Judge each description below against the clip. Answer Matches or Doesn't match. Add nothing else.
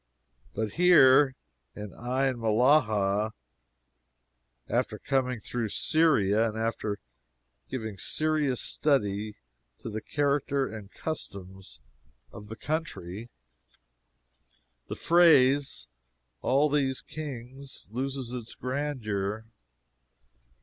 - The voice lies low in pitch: Matches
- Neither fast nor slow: Doesn't match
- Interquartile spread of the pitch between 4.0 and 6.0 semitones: Matches